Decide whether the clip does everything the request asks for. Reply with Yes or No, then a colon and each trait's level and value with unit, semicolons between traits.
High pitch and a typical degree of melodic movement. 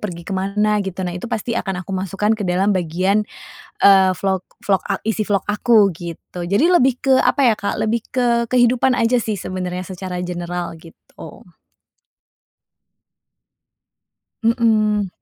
Yes: high, 200 Hz; average, 3.8 semitones